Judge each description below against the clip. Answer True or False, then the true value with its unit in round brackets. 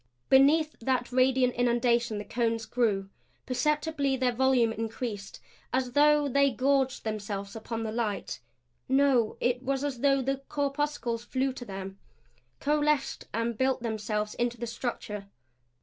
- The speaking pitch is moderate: False (245 Hz)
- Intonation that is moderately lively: True (3.2 semitones)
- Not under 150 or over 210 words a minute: False (135 wpm)